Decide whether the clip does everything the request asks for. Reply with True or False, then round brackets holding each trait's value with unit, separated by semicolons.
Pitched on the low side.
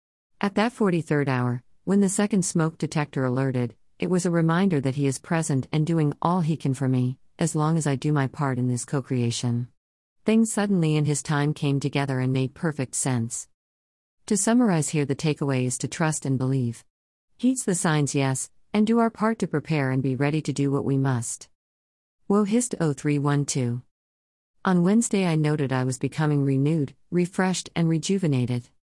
False (145 Hz)